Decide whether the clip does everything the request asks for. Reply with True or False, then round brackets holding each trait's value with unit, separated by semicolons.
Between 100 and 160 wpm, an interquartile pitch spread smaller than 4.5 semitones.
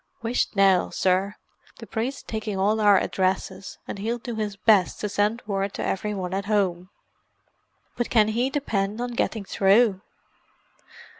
True (155 wpm; 2.4 semitones)